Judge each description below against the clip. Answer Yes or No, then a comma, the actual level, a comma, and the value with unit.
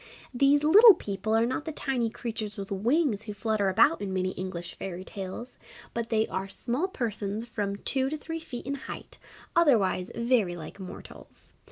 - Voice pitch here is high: Yes, high, 220 Hz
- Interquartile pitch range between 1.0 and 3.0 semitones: No, average, 5.3 semitones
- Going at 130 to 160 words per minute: No, average, 175 wpm